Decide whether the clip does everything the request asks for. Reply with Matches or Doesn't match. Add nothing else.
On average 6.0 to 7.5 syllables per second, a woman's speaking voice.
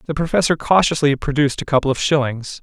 Doesn't match